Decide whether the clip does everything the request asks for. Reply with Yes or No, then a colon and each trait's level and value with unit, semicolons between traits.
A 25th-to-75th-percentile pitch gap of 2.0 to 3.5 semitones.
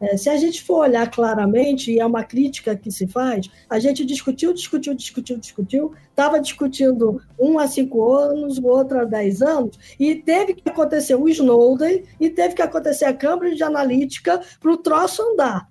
No: average, 4.7 semitones